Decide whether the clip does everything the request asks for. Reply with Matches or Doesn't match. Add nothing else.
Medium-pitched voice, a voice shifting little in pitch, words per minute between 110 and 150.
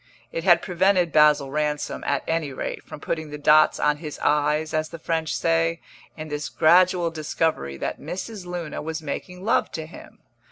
Doesn't match